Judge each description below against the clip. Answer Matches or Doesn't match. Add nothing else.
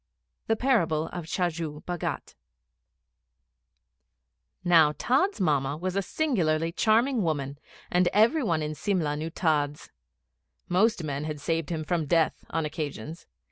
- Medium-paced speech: Doesn't match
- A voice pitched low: Doesn't match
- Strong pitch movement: Doesn't match